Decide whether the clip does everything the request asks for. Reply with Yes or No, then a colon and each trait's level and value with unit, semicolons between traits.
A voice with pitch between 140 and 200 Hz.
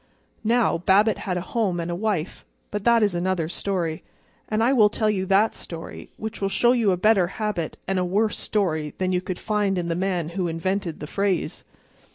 Yes: high, 190 Hz